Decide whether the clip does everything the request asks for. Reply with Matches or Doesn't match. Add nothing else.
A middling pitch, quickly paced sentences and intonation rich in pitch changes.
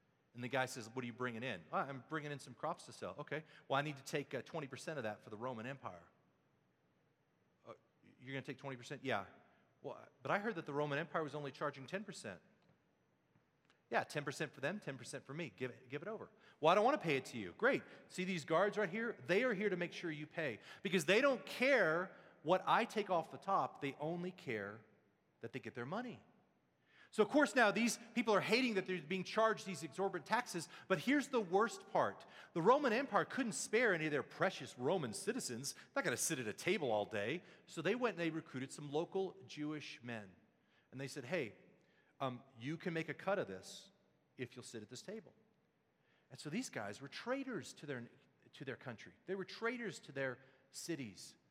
Matches